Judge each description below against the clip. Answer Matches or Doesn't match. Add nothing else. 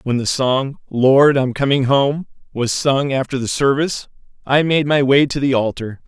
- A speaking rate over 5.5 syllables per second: Doesn't match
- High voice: Doesn't match